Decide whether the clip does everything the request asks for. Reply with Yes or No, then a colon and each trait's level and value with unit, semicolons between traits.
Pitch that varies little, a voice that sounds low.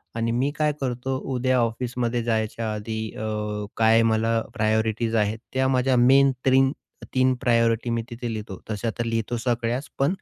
Yes: narrow, 2.3 semitones; low, 115 Hz